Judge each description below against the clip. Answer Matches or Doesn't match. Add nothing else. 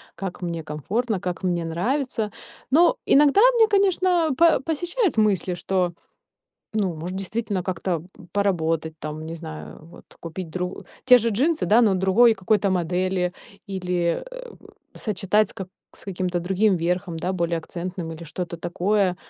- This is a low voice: Doesn't match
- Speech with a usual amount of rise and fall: Matches